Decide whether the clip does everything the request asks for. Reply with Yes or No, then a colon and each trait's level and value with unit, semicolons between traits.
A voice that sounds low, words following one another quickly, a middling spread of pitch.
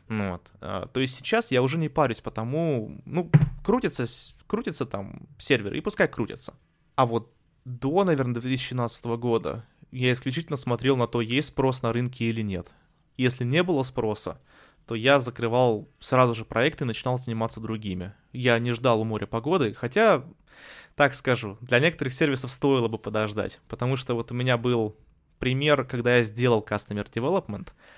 Yes: low, 125 Hz; fast, 165 wpm; average, 3.1 semitones